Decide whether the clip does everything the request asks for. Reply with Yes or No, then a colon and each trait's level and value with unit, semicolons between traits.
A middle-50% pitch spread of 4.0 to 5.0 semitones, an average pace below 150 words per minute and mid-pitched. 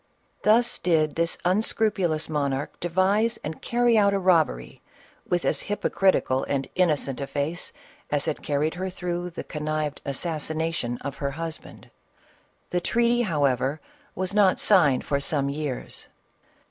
Yes: average, 4.6 semitones; average, 140 wpm; medium, 165 Hz